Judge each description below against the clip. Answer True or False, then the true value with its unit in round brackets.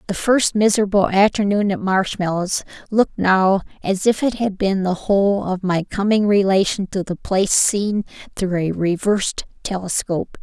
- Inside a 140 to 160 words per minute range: True (155 wpm)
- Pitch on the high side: True (195 Hz)